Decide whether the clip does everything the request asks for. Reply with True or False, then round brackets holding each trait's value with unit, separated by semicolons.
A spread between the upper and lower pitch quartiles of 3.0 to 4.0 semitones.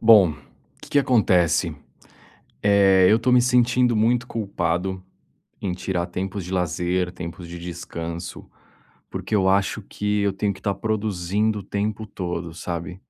True (3.4 semitones)